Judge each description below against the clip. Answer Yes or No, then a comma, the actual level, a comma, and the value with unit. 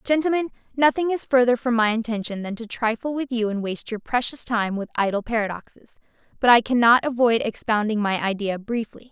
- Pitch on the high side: Yes, high, 235 Hz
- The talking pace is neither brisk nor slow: Yes, average, 185 wpm